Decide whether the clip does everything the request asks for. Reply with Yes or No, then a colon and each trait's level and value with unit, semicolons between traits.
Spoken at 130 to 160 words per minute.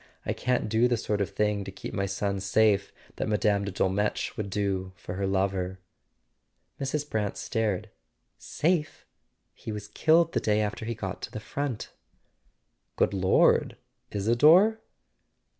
Yes: average, 145 wpm